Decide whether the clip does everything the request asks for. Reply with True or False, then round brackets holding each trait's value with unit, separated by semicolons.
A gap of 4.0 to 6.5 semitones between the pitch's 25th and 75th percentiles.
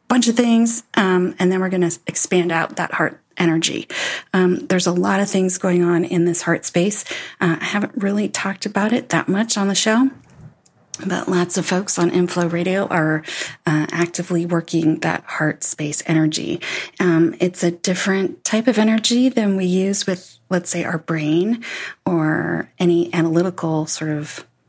False (2.9 semitones)